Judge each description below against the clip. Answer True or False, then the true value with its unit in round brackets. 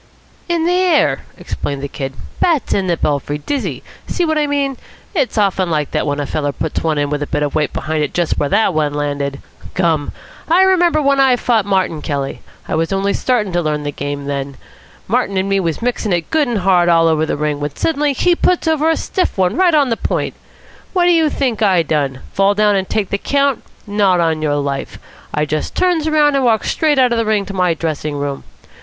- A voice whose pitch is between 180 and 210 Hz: True (190 Hz)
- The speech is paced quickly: True (230 wpm)